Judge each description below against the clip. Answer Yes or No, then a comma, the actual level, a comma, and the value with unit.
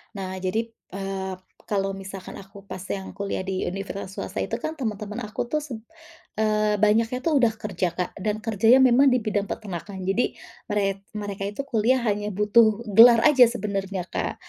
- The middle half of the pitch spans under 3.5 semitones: Yes, average, 2.8 semitones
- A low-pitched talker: No, high, 210 Hz